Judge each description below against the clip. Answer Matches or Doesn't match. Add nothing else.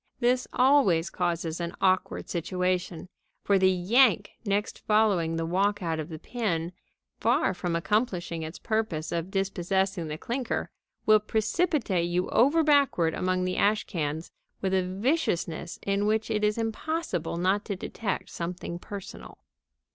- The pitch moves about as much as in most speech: Matches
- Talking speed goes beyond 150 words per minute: Doesn't match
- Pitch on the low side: Doesn't match